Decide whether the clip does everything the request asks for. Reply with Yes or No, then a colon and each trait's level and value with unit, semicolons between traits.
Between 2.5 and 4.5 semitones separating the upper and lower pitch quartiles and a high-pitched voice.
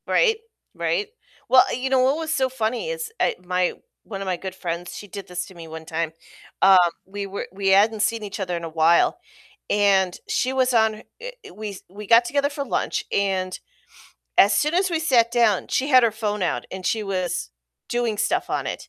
No: wide, 5.4 semitones; high, 210 Hz